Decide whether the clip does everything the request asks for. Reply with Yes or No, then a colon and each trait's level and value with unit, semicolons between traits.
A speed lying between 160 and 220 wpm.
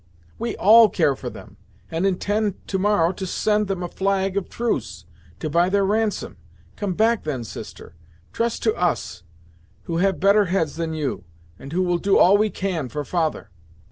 Yes: average, 180 wpm